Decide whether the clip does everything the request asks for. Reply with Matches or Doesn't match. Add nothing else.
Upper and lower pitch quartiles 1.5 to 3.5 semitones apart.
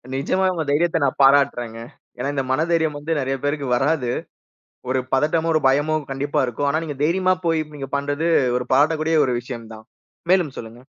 Matches